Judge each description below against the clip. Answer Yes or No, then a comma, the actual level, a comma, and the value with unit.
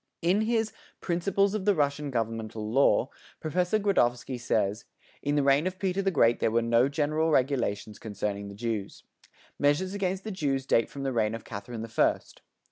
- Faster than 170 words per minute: Yes, average, 180 wpm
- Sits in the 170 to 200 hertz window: No, medium, 140 Hz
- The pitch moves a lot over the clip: Yes, wide, 8.0 semitones